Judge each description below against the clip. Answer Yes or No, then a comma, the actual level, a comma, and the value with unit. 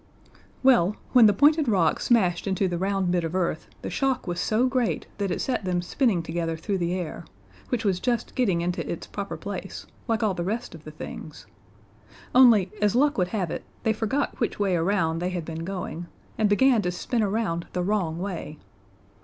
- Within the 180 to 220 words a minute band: Yes, average, 200 wpm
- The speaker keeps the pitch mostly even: No, average, 4.6 semitones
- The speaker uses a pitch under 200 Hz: Yes, high, 190 Hz